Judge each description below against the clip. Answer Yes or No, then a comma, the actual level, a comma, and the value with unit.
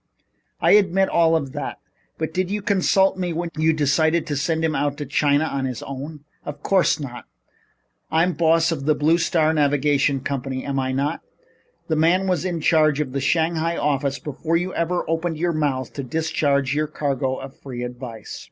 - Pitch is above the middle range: No, medium, 155 Hz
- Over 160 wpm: Yes, average, 190 wpm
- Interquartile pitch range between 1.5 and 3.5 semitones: Yes, average, 3.1 semitones